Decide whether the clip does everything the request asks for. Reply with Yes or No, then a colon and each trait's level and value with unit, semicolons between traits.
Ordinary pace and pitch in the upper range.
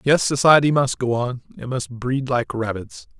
No: average, 190 wpm; low, 130 Hz